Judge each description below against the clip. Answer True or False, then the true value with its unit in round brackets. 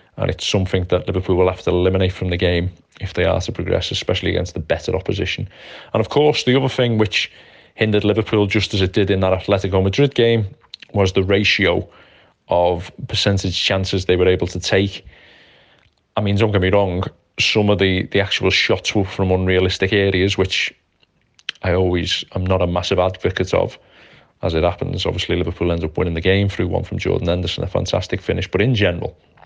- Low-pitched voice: True (95 Hz)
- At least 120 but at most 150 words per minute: False (200 wpm)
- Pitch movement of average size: False (2.0 semitones)